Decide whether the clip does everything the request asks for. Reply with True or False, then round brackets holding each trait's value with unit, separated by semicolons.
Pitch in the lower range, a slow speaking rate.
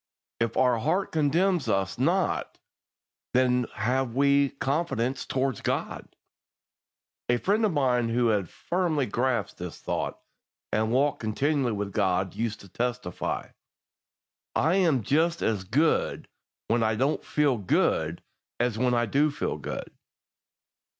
True (125 Hz; 130 wpm)